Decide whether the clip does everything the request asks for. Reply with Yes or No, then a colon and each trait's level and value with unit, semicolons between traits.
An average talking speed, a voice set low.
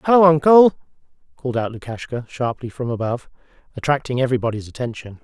No: slow, 125 wpm; low, 130 Hz